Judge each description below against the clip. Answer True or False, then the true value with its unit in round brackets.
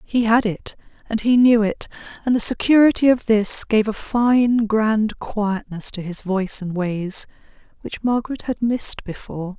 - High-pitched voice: True (220 Hz)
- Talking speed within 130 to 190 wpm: True (170 wpm)